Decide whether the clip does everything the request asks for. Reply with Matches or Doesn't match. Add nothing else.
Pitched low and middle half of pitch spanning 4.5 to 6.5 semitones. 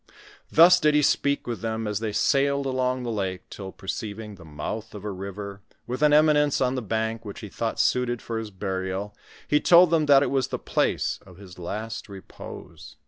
Matches